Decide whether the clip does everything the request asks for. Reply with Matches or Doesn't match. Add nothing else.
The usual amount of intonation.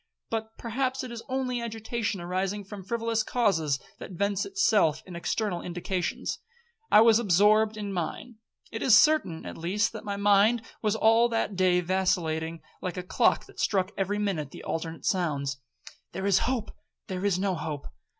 Matches